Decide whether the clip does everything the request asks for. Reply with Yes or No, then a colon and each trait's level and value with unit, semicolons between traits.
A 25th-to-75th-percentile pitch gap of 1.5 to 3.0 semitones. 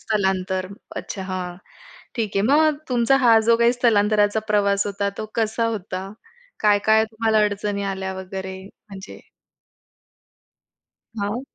Yes: narrow, 2.6 semitones